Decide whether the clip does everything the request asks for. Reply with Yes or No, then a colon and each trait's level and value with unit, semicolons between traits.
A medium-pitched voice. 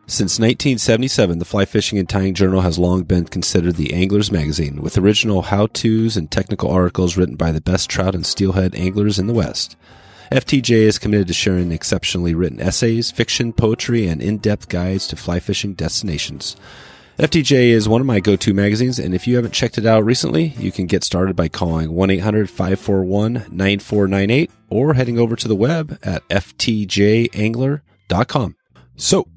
No: low, 100 Hz